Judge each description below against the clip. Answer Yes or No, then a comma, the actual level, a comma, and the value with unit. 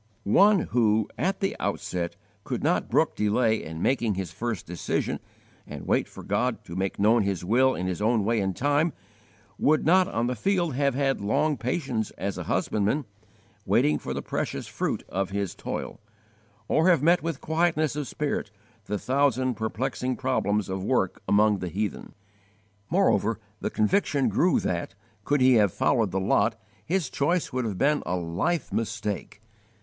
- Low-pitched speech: Yes, low, 115 Hz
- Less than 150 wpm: No, average, 170 wpm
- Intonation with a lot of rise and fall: Yes, wide, 6.1 semitones